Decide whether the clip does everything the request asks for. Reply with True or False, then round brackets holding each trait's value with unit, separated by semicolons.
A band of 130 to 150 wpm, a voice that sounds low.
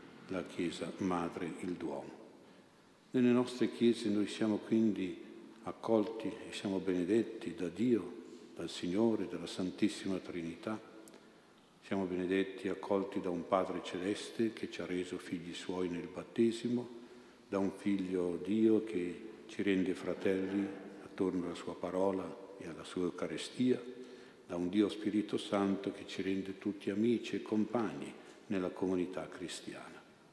True (135 wpm; 100 Hz)